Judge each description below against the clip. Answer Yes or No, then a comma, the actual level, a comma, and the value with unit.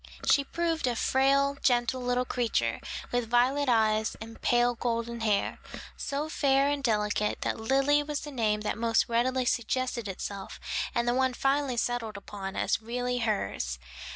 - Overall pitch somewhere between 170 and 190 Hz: No, high, 245 Hz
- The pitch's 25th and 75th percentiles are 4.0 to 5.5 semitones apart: No, average, 3.2 semitones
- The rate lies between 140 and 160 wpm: Yes, average, 155 wpm